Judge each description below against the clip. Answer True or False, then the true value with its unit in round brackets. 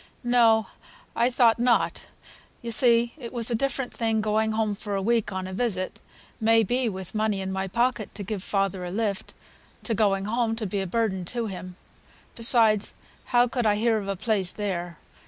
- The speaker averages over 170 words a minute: True (190 wpm)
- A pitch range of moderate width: True (3.2 semitones)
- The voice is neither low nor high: False (220 Hz)